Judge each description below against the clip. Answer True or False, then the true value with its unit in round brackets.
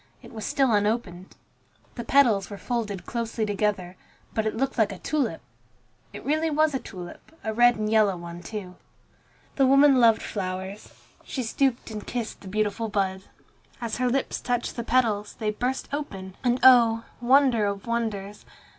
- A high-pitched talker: True (225 Hz)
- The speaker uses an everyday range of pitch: True (3.6 semitones)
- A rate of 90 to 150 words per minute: False (165 wpm)